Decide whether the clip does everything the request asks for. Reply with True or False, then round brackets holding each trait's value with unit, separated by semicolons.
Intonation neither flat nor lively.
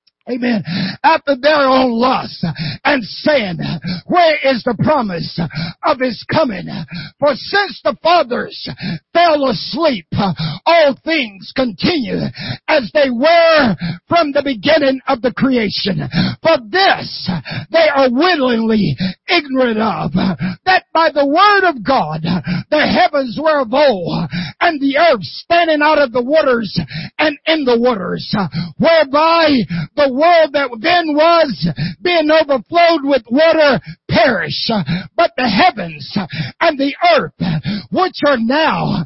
False (8.9 semitones)